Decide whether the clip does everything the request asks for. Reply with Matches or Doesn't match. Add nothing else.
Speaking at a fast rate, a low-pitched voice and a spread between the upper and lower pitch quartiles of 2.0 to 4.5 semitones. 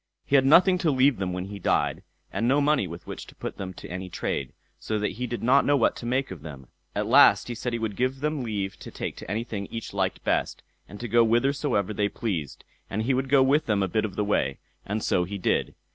Doesn't match